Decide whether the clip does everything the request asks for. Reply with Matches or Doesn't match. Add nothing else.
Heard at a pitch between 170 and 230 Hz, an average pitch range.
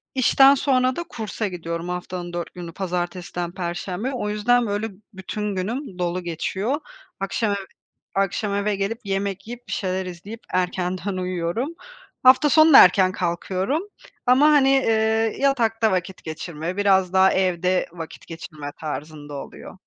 Matches